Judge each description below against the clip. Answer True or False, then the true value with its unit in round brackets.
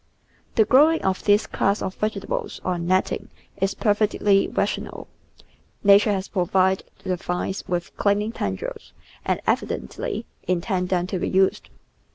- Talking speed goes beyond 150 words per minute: False (140 wpm)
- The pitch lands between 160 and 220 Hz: True (190 Hz)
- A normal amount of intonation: False (2.1 semitones)